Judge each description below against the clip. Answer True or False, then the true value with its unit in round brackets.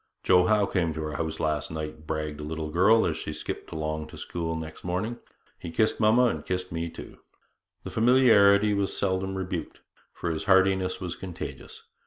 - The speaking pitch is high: False (90 Hz)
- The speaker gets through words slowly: False (185 wpm)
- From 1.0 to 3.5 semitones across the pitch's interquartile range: False (4.1 semitones)